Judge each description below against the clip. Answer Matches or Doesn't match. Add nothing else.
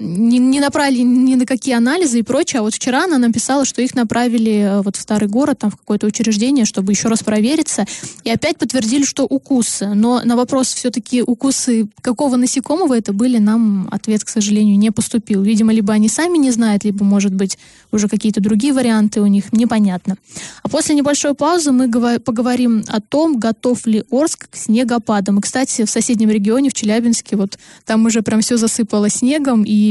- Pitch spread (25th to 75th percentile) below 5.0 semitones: Matches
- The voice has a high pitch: Matches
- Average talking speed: Doesn't match